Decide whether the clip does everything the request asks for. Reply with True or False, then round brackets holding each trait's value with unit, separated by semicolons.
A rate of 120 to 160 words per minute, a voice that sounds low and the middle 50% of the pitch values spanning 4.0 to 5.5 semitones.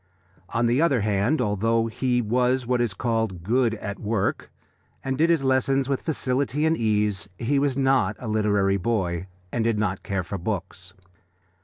False (170 wpm; 115 Hz; 4.3 semitones)